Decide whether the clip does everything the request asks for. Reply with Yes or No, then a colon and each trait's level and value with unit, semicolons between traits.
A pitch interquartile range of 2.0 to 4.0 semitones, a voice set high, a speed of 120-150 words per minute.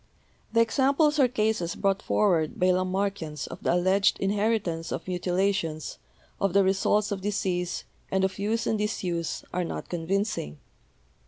Yes: average, 2.9 semitones; high, 195 Hz; average, 145 wpm